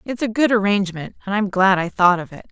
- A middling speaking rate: No, fast, 260 wpm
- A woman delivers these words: Yes, female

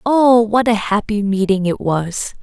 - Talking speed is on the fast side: No, average, 175 wpm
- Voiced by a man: No, female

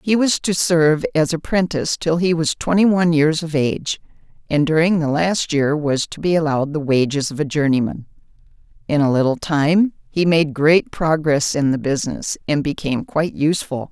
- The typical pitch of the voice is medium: Yes, medium, 155 Hz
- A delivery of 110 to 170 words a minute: No, average, 185 wpm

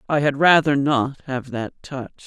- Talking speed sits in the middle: Yes, average, 185 wpm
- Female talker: Yes, female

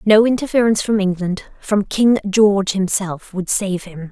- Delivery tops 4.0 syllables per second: Yes, 4.7 syllables/s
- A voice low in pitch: No, high, 200 Hz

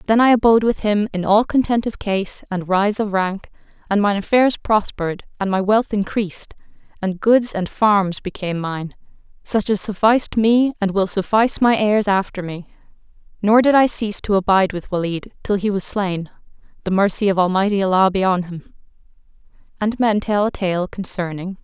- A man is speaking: No, female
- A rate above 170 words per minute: Yes, average, 180 wpm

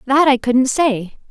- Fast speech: No, average, 185 wpm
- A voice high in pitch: Yes, very high, 260 Hz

